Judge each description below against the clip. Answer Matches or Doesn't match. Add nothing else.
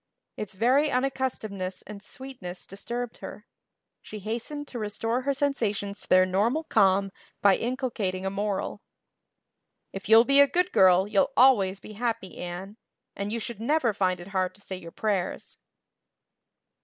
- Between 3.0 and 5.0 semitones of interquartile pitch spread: Matches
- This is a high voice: Matches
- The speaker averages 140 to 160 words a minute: Matches